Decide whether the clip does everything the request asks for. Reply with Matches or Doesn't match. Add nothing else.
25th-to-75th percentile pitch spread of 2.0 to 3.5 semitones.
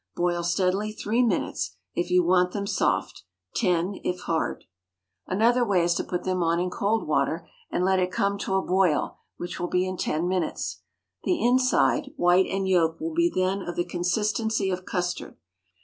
Matches